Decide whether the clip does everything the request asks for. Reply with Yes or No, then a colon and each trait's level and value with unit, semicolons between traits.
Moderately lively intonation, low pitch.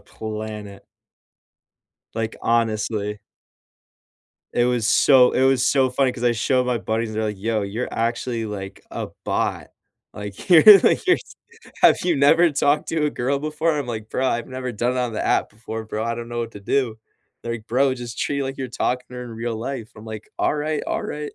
Yes: average, 3.3 semitones; low, 120 Hz